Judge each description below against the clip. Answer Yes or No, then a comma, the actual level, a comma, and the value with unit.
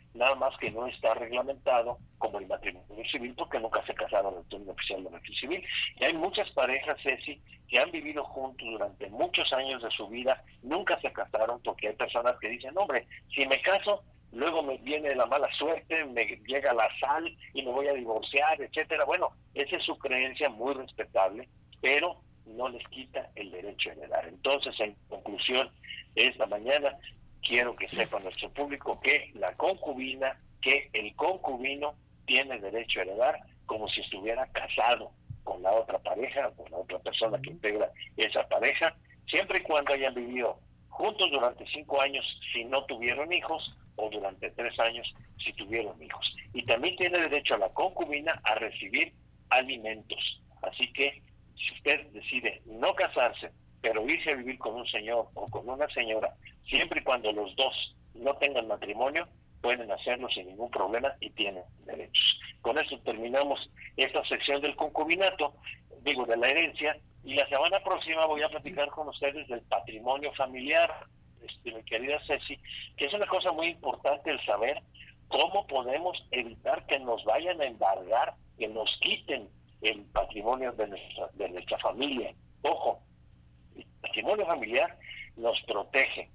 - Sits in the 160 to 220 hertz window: No, low, 130 Hz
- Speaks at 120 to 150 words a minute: No, average, 165 wpm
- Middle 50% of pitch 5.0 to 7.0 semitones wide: No, average, 4.4 semitones